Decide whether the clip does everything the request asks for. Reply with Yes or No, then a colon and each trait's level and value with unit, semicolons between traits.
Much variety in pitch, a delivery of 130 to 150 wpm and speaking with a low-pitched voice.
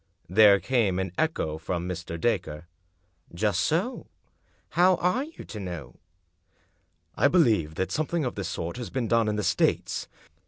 No: wide, 7.3 semitones; average, 165 wpm; low, 105 Hz